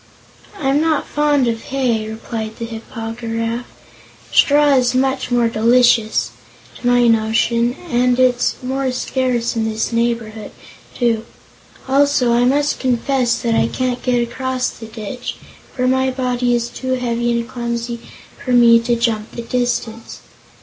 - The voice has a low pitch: No, high, 240 Hz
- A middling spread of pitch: No, narrow, 1.8 semitones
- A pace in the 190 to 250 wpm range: No, average, 150 wpm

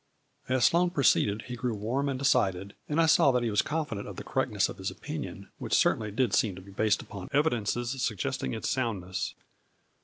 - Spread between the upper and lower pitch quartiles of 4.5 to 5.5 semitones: Yes, average, 4.8 semitones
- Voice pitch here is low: Yes, low, 115 Hz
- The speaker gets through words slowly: No, fast, 205 wpm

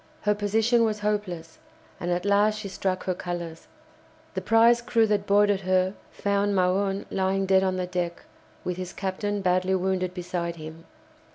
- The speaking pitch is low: No, high, 190 Hz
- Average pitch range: No, narrow, 2.2 semitones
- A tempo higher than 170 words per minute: No, average, 165 wpm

